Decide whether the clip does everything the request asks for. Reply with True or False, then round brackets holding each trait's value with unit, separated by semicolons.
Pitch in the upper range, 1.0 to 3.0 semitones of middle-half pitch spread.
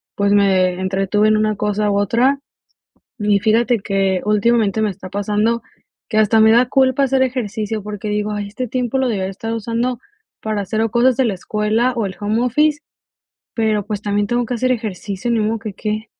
True (215 Hz; 2.5 semitones)